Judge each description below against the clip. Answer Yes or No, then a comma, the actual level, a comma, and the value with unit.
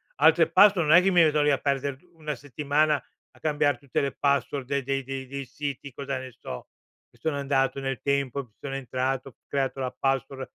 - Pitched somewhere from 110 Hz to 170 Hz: Yes, medium, 140 Hz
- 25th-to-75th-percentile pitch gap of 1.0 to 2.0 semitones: Yes, narrow, 1.4 semitones